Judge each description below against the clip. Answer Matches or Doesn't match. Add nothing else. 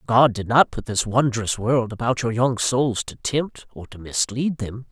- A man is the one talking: Matches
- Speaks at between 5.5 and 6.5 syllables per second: Doesn't match